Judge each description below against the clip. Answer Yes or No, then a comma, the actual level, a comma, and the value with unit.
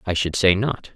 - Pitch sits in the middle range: No, very low, 95 Hz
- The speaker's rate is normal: No, fast, 250 wpm